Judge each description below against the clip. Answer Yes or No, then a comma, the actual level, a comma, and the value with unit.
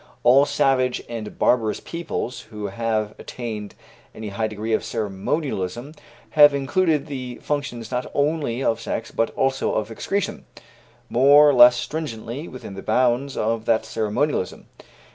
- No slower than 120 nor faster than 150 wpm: Yes, average, 140 wpm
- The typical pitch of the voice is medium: No, low, 120 Hz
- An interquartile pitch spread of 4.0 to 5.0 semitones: Yes, average, 4.3 semitones